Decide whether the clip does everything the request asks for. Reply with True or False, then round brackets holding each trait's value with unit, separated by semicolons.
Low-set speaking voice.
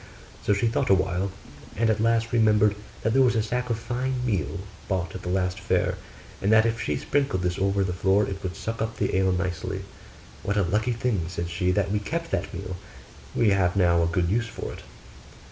True (100 Hz)